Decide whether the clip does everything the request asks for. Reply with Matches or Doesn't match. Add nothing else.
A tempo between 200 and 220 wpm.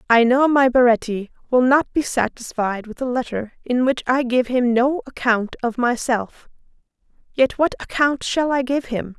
Doesn't match